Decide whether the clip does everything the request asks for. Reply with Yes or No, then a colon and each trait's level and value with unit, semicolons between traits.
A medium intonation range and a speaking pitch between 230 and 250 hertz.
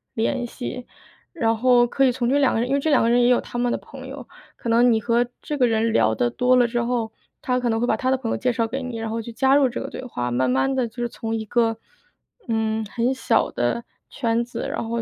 No: narrow, 2.1 semitones; high, 240 Hz